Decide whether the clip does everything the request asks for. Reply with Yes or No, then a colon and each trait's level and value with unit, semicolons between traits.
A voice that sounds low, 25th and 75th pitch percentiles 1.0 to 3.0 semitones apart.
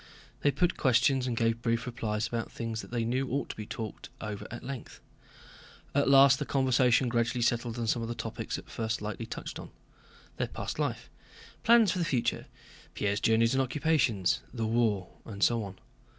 Yes: low, 120 Hz; average, 2.7 semitones